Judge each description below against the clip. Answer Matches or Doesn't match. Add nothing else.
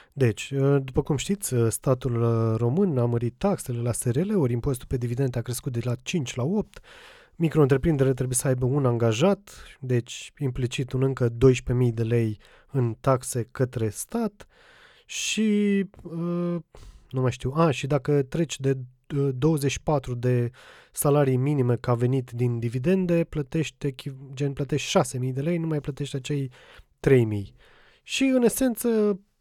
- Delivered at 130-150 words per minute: Matches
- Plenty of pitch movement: Doesn't match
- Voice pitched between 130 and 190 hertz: Matches